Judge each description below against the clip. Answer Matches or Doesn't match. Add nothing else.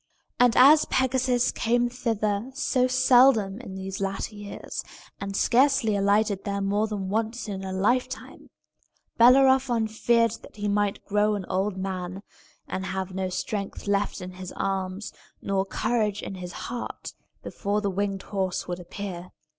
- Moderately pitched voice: Doesn't match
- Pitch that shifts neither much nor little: Matches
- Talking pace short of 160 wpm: Matches